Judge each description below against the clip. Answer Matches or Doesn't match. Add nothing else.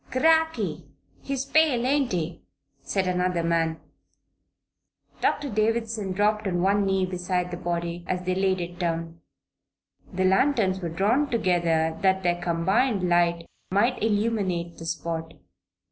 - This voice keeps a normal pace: Doesn't match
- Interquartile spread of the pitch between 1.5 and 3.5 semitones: Doesn't match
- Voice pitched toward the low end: Doesn't match